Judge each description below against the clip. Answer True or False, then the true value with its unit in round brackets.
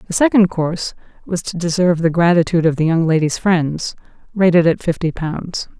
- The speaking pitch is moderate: True (170 Hz)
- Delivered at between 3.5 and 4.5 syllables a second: False (5.5 syllables/s)